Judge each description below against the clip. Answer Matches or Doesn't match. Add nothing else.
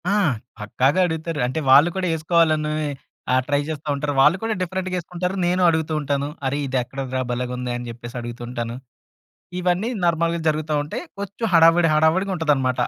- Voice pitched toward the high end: Doesn't match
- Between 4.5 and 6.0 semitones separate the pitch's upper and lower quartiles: Matches